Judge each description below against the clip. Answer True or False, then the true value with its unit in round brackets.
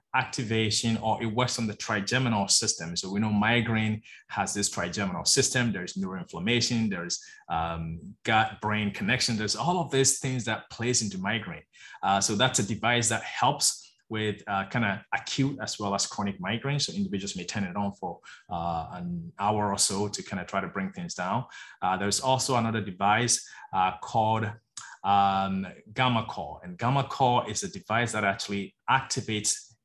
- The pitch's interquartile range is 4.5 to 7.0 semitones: False (3.5 semitones)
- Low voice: True (110 Hz)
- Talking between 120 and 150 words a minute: False (175 wpm)